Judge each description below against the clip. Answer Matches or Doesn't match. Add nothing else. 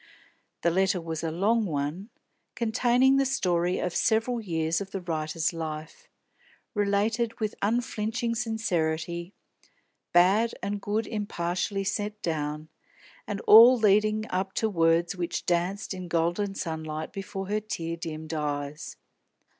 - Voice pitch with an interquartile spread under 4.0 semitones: Doesn't match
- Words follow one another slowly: Matches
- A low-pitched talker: Doesn't match